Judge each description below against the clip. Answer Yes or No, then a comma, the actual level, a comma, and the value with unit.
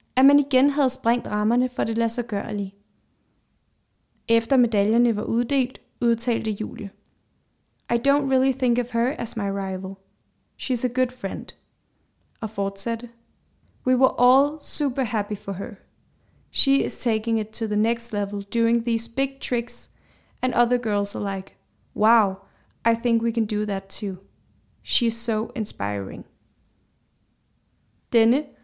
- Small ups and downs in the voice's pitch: No, average, 3.3 semitones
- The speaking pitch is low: No, high, 230 Hz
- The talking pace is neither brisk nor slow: No, slow, 140 wpm